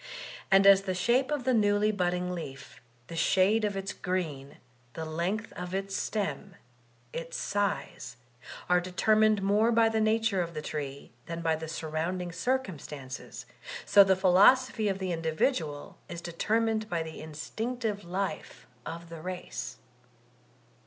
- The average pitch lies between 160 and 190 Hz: Yes, medium, 185 Hz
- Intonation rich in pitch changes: No, average, 4.4 semitones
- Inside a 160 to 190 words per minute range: No, average, 150 wpm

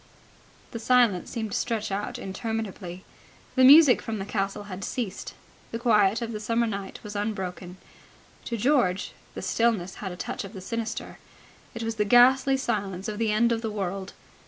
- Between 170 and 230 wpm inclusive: Yes, average, 180 wpm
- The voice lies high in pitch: Yes, high, 215 Hz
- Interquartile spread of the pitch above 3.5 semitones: No, average, 3.1 semitones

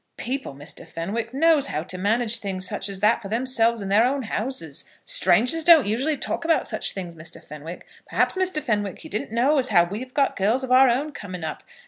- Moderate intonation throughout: No, wide, 5.7 semitones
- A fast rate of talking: Yes, fast, 215 wpm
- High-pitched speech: Yes, high, 225 Hz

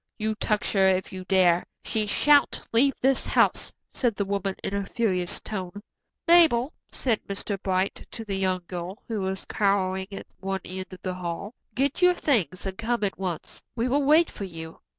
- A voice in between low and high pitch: No, high, 200 Hz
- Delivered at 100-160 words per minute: No, average, 190 wpm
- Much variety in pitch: No, average, 3.8 semitones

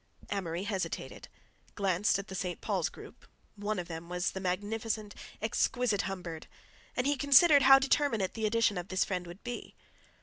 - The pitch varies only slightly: No, average, 4.0 semitones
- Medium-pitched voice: No, high, 205 Hz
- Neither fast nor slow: Yes, average, 155 wpm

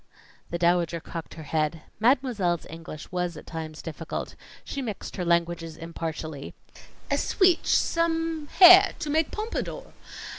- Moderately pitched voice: Yes, medium, 175 Hz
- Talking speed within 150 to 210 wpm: No, slow, 135 wpm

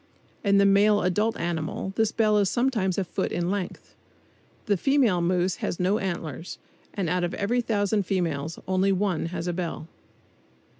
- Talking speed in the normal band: Yes, average, 165 wpm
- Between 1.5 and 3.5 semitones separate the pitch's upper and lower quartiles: Yes, average, 2.9 semitones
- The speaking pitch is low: No, high, 190 Hz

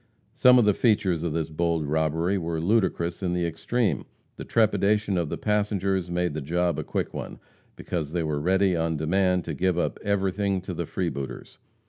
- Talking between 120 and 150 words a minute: No, average, 185 wpm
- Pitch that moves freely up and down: No, average, 3.3 semitones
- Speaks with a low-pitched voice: Yes, very low, 90 Hz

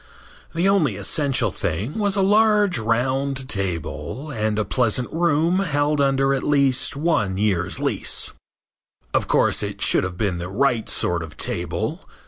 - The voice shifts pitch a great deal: Yes, wide, 6.9 semitones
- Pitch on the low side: Yes, low, 130 Hz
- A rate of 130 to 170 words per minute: Yes, average, 150 wpm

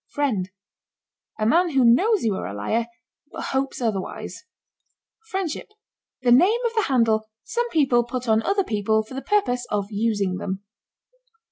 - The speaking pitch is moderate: No, high, 240 Hz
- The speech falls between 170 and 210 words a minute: No, average, 155 wpm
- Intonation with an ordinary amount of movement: No, wide, 6.8 semitones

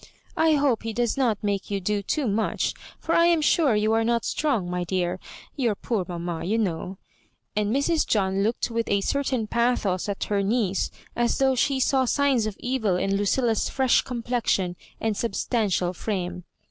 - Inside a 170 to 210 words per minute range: Yes, average, 185 wpm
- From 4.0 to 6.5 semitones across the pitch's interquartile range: Yes, average, 4.4 semitones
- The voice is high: Yes, high, 220 Hz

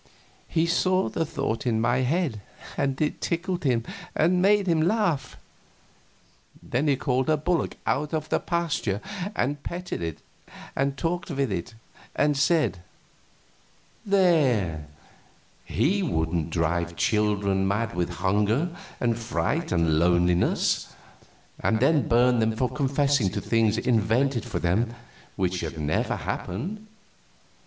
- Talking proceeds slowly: Yes, slow, 130 wpm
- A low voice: Yes, low, 125 Hz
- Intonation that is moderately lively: No, wide, 8.2 semitones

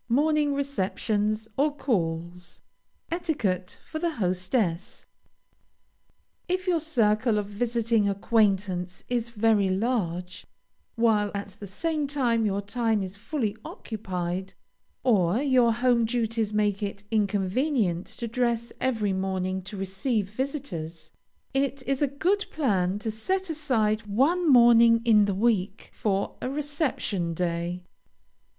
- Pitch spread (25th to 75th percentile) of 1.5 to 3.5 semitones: No, average, 5.1 semitones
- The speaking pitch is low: No, high, 220 Hz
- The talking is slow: Yes, slow, 120 wpm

